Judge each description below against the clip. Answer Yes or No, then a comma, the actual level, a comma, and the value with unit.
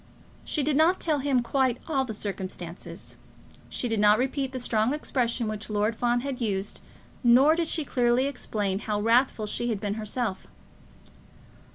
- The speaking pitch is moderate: No, high, 240 Hz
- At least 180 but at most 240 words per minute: No, average, 165 wpm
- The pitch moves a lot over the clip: No, average, 4.1 semitones